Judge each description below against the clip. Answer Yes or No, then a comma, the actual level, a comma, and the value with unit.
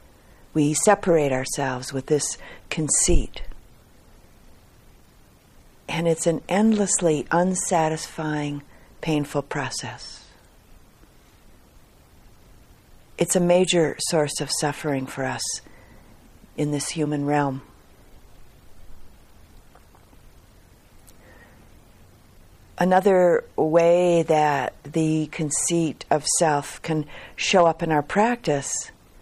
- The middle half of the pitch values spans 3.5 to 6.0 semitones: Yes, average, 5.1 semitones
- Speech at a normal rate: No, slow, 80 wpm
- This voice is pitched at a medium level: Yes, medium, 150 Hz